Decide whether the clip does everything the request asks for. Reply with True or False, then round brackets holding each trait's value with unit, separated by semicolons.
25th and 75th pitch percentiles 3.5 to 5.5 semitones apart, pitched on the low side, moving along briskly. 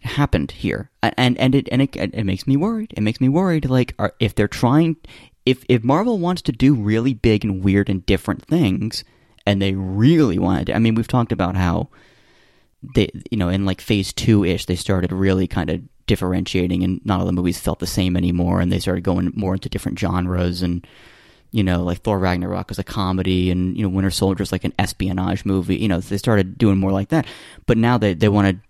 True (4.3 semitones; 100 Hz; 225 wpm)